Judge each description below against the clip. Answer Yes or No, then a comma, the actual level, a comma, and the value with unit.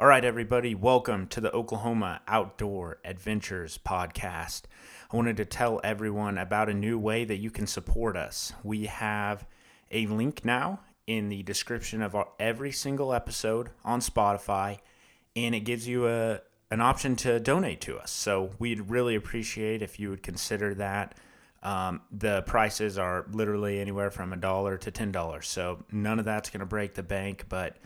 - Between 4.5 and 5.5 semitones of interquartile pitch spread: No, average, 2.7 semitones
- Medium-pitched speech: No, low, 105 Hz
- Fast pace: No, average, 175 wpm